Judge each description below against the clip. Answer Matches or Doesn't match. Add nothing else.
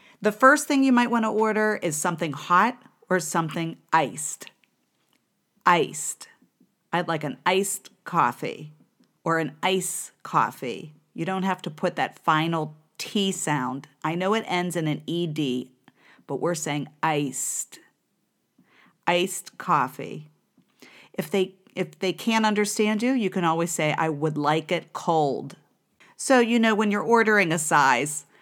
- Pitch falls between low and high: Matches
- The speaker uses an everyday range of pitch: Matches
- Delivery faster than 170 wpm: Doesn't match